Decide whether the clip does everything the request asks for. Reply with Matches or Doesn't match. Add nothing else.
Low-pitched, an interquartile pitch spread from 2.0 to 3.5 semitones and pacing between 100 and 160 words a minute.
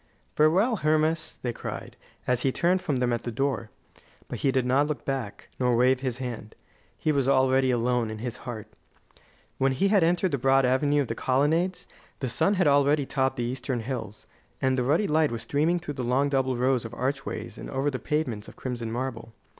Doesn't match